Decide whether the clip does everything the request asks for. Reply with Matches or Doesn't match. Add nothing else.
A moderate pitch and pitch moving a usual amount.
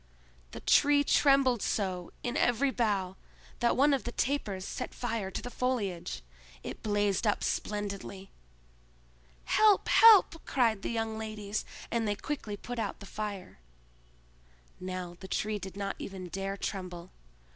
Doesn't match